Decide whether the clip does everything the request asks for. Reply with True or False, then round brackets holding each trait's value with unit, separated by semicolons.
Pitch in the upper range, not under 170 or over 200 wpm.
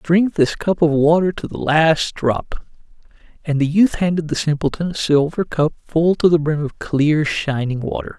False (155 Hz; 190 wpm)